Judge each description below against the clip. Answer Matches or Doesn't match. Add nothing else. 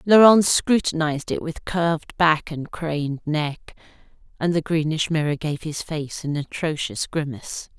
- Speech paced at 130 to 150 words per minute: Matches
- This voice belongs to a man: Doesn't match